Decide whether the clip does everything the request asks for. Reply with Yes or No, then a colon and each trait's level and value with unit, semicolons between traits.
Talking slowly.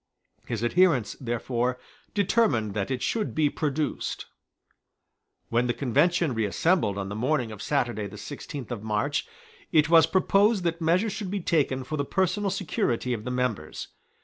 No: average, 155 wpm